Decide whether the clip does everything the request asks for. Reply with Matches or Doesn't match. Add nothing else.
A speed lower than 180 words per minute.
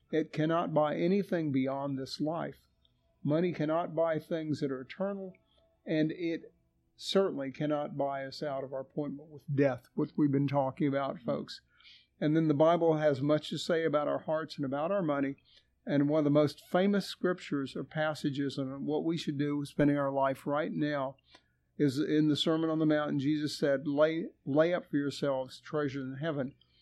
Doesn't match